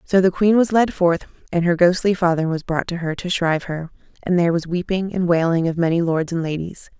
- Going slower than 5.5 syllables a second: No, 5.7 syllables/s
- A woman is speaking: Yes, female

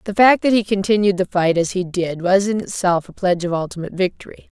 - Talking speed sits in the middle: No, fast, 235 wpm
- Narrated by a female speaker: Yes, female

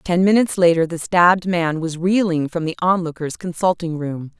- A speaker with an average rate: Yes, average, 180 wpm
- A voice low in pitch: No, medium, 170 Hz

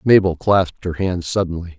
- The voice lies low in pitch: Yes, very low, 90 Hz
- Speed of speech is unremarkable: Yes, average, 170 wpm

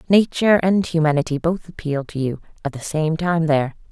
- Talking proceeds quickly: No, average, 185 wpm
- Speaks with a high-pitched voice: No, medium, 160 Hz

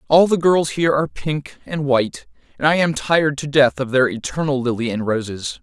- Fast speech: Yes, fast, 215 wpm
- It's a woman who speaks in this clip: No, male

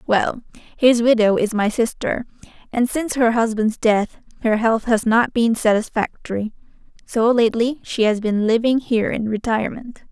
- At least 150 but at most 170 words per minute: Yes, average, 155 wpm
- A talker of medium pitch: No, high, 230 Hz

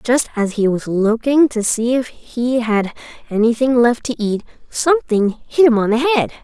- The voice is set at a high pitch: Yes, high, 240 Hz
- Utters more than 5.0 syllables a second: No, 4.6 syllables/s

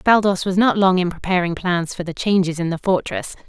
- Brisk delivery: Yes, fast, 225 wpm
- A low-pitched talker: No, medium, 185 Hz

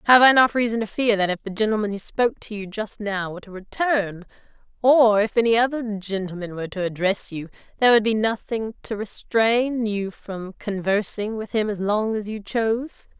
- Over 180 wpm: Yes, average, 200 wpm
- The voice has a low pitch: No, high, 215 Hz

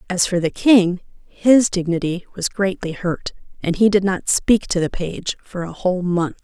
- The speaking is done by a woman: Yes, female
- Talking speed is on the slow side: No, average, 195 wpm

